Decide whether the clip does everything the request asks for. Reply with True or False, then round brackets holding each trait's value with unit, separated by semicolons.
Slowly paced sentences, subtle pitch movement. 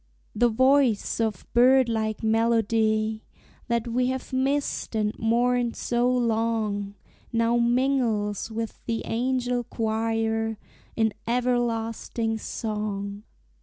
True (100 wpm; 1.9 semitones)